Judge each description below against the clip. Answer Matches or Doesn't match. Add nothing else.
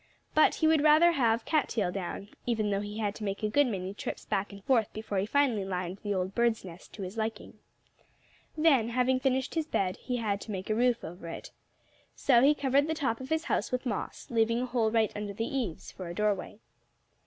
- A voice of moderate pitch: Doesn't match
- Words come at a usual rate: Doesn't match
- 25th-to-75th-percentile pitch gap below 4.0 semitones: Doesn't match